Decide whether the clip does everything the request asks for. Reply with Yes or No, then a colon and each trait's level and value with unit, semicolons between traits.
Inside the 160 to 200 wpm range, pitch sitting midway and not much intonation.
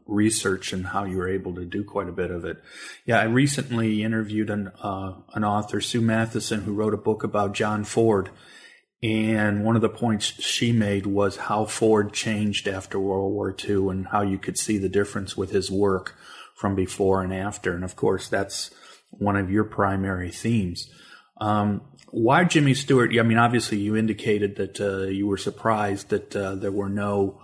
No: average, 190 wpm; low, 105 Hz; narrow, 2.1 semitones